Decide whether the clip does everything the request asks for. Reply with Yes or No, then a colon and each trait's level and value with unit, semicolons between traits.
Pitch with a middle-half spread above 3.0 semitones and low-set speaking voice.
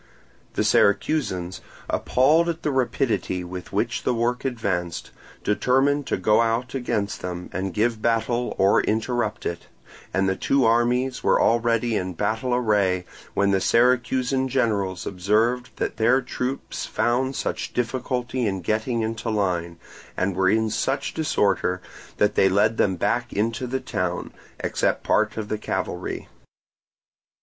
Yes: average, 4.3 semitones; low, 115 Hz